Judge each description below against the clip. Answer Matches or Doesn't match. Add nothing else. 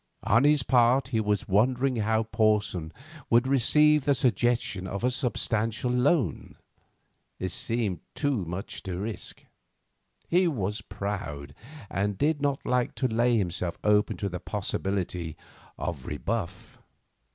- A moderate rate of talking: Doesn't match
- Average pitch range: Matches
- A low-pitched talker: Matches